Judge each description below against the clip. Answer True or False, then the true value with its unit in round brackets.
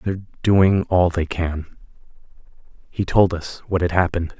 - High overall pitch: False (90 Hz)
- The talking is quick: False (150 wpm)